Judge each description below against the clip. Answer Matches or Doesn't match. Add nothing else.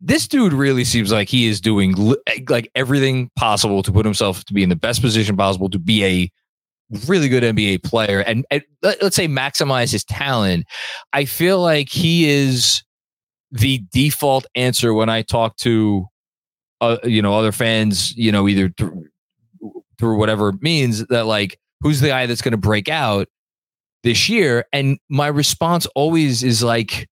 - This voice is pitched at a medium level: Doesn't match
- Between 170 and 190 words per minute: Matches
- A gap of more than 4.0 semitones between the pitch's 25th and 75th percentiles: Matches